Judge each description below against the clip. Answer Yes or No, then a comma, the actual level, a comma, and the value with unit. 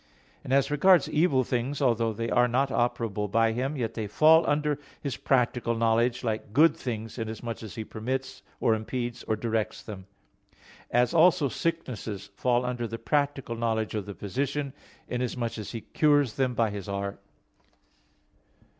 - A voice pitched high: No, low, 120 Hz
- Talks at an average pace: Yes, average, 160 wpm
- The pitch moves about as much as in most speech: Yes, average, 3.4 semitones